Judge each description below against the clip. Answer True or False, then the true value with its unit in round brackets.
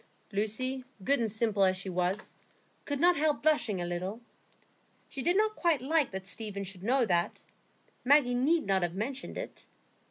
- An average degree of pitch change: False (6.6 semitones)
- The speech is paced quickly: False (170 wpm)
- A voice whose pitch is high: True (230 Hz)